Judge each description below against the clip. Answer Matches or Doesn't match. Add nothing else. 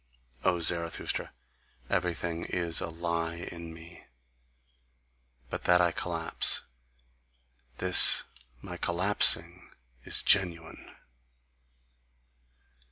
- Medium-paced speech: Doesn't match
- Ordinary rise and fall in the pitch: Doesn't match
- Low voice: Matches